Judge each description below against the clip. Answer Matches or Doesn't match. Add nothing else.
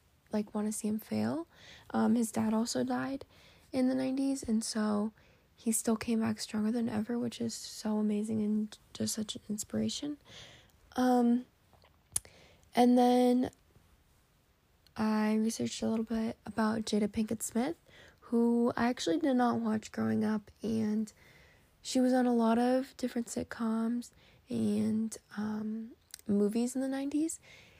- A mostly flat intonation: Matches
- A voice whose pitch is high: Matches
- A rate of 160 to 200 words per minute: Doesn't match